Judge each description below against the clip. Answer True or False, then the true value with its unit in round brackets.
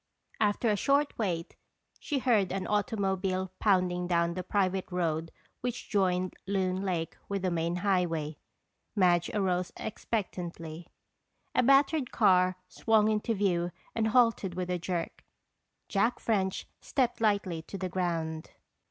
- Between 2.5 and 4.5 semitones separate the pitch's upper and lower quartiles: True (3.0 semitones)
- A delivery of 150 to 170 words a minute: False (135 wpm)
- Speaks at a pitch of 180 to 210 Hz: True (185 Hz)